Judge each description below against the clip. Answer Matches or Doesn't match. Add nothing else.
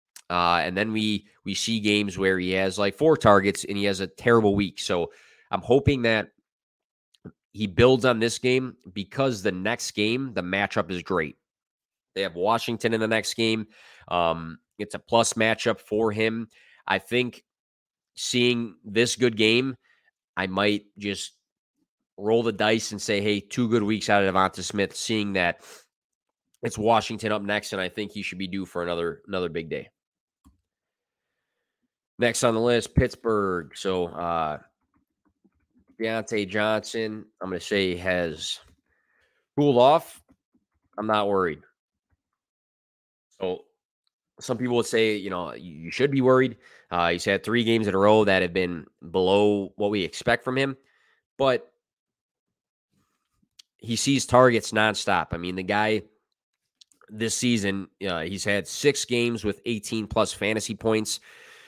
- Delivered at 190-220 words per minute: Doesn't match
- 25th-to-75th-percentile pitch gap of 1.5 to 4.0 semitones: Matches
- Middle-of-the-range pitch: Doesn't match